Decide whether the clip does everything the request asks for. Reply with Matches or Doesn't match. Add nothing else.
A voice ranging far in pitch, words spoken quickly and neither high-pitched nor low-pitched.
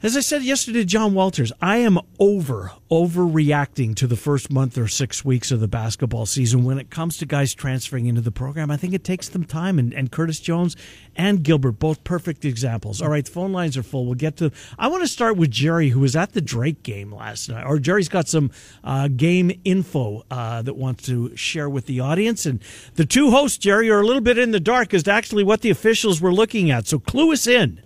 Matches